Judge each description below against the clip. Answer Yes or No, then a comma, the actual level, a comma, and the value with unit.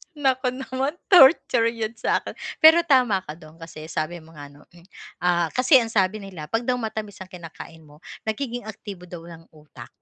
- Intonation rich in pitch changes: Yes, wide, 7.1 semitones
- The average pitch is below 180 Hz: No, high, 195 Hz